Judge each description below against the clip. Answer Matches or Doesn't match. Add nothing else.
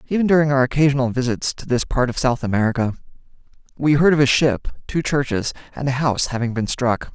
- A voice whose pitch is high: Doesn't match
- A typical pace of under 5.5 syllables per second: Doesn't match